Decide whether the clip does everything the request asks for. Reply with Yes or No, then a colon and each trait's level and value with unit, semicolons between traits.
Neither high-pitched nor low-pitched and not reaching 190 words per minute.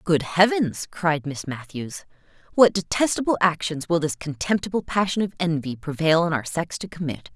Yes: medium, 170 Hz; average, 165 wpm